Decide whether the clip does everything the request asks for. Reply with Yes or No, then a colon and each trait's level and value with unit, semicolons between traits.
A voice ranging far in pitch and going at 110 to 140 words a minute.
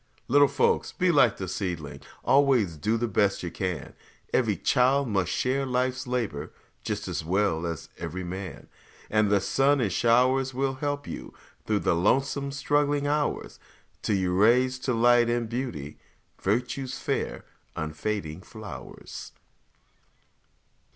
Yes: wide, 6.1 semitones; slow, 135 wpm